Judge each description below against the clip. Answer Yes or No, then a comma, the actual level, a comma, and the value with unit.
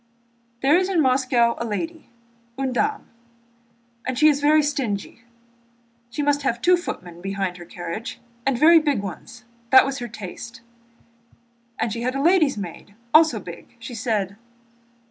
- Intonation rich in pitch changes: Yes, wide, 5.7 semitones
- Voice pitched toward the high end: Yes, very high, 250 Hz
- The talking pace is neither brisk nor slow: Yes, average, 155 wpm